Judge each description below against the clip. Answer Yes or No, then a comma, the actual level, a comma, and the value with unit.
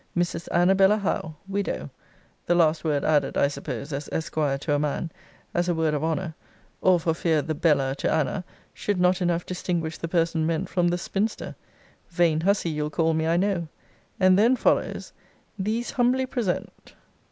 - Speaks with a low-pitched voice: No, medium, 170 Hz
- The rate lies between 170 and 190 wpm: Yes, average, 175 wpm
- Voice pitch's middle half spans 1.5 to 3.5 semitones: Yes, average, 2.9 semitones